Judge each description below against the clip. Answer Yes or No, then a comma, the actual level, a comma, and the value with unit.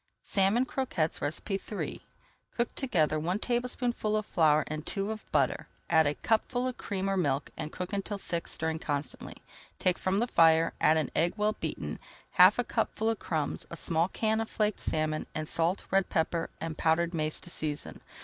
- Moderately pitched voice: Yes, medium, 175 Hz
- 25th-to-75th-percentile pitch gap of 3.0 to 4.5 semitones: No, average, 5.2 semitones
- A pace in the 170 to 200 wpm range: Yes, average, 180 wpm